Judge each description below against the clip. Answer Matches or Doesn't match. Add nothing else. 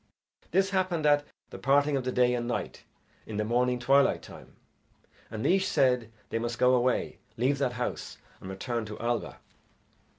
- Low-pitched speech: Matches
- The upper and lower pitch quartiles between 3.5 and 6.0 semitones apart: Doesn't match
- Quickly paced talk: Doesn't match